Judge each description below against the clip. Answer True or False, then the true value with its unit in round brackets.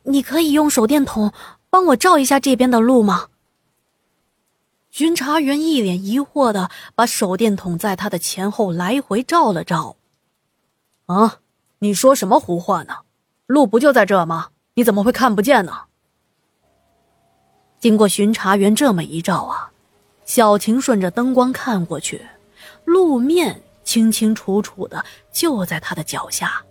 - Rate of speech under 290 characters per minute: True (210 characters per minute)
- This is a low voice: False (225 Hz)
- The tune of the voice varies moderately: False (5.8 semitones)